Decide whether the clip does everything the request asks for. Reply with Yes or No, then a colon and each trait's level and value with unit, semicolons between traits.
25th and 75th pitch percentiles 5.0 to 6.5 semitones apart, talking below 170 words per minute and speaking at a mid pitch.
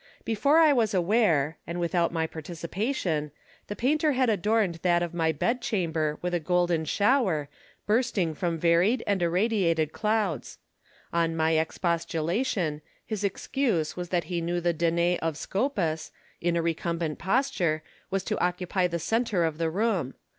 No: average, 4.4 semitones; average, 155 wpm; medium, 175 Hz